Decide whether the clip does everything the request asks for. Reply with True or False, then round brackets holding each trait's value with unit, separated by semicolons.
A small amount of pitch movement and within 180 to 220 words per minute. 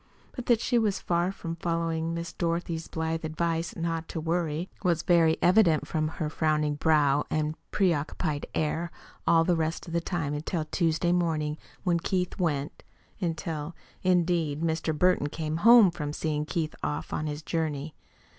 False (2.0 semitones; 160 wpm)